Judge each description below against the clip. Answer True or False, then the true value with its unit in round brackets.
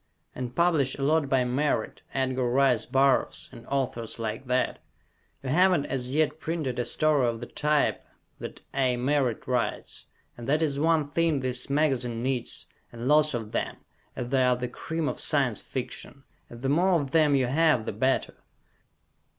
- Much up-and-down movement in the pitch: False (3.4 semitones)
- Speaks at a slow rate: False (175 wpm)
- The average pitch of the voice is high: False (135 Hz)